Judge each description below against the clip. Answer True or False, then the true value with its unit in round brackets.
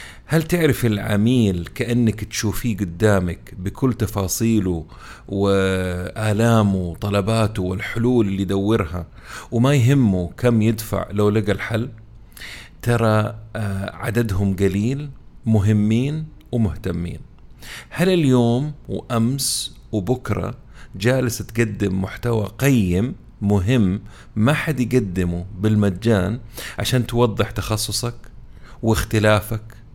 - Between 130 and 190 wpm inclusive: False (85 wpm)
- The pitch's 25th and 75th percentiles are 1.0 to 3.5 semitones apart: True (3.1 semitones)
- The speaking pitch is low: True (110 Hz)